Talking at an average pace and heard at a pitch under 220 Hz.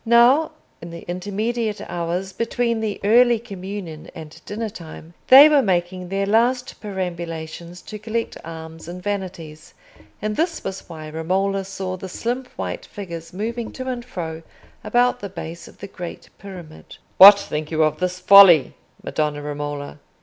Yes: average, 155 wpm; high, 190 Hz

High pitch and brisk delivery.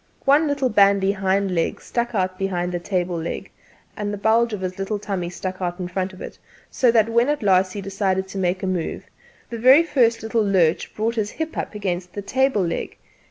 Yes: high, 195 Hz; fast, 215 wpm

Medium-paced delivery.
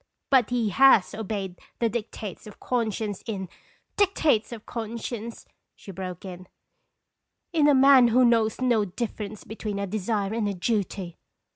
Yes: average, 160 wpm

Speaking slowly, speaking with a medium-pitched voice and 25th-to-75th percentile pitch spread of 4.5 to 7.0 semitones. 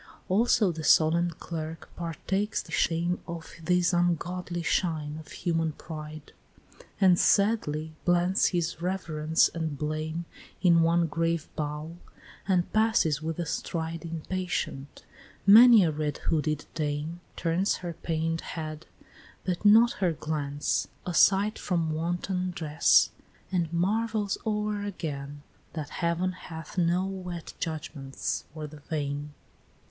No: slow, 125 wpm; medium, 165 Hz; average, 2.7 semitones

